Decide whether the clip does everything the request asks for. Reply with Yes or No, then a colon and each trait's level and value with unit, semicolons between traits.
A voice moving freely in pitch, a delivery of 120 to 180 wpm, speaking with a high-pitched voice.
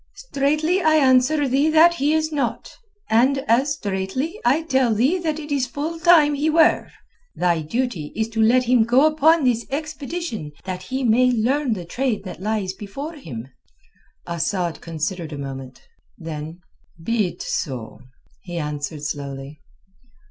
Yes: wide, 9.0 semitones; average, 155 wpm; high, 245 Hz